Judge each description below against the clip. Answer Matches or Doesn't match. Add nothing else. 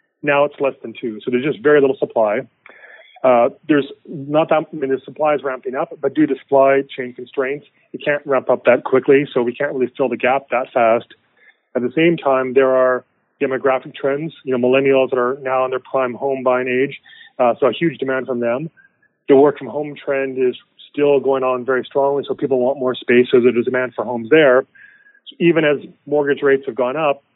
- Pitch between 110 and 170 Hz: Matches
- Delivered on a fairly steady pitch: Matches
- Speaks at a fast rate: Matches